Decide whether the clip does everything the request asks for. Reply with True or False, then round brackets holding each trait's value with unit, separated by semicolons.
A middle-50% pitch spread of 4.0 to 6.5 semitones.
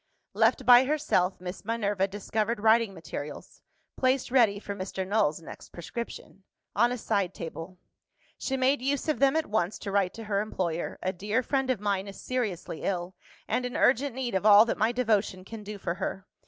True (4.5 semitones)